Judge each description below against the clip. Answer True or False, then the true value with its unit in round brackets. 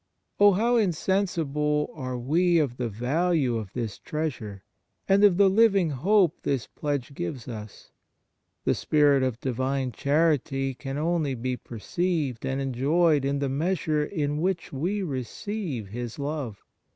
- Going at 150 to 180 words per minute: False (140 wpm)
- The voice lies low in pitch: False (145 Hz)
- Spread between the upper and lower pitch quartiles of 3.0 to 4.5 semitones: False (5.2 semitones)